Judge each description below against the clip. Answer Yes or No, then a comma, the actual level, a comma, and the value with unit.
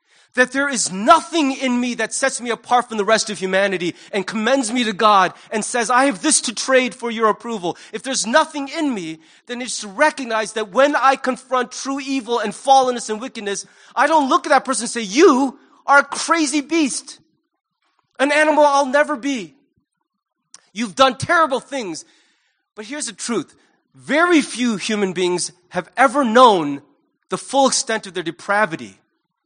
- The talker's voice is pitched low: No, high, 245 Hz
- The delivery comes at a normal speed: Yes, average, 180 wpm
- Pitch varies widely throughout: No, average, 4.6 semitones